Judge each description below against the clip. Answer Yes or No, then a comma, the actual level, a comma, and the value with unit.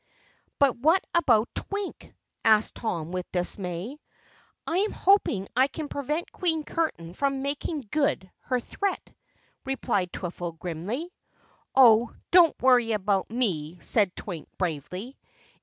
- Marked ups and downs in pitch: Yes, wide, 8.2 semitones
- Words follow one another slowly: Yes, slow, 125 wpm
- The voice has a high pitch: Yes, high, 235 Hz